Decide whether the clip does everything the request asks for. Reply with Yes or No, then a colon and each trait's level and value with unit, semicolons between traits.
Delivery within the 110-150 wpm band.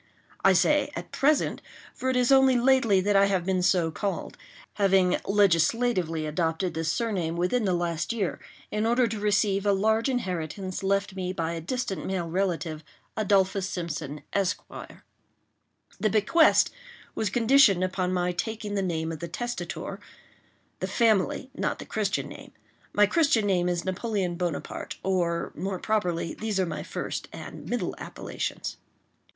Yes: average, 145 wpm